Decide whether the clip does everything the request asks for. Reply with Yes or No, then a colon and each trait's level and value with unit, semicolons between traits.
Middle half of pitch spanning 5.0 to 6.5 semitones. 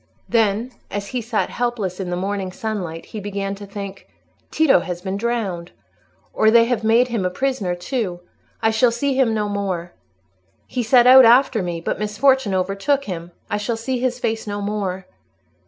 No: average, 3.9 semitones